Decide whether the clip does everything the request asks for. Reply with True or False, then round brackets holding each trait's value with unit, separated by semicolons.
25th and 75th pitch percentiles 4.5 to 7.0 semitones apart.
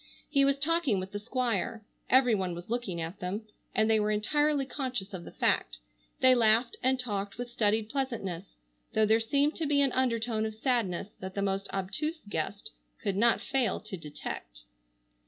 True (4.8 semitones)